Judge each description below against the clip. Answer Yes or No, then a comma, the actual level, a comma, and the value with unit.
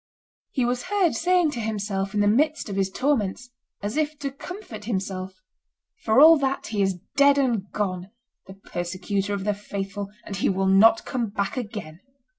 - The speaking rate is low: No, average, 185 wpm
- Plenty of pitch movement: Yes, wide, 5.7 semitones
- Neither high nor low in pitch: No, high, 210 Hz